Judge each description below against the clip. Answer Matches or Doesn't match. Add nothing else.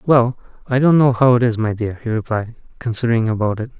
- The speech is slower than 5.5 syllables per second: Doesn't match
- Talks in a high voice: Doesn't match